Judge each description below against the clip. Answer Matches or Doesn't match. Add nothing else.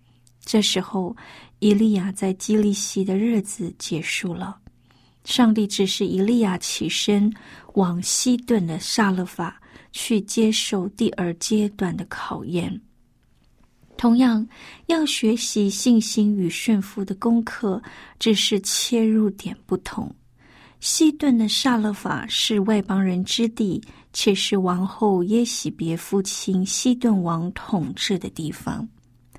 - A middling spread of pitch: Matches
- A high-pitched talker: Matches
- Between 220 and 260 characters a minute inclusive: Doesn't match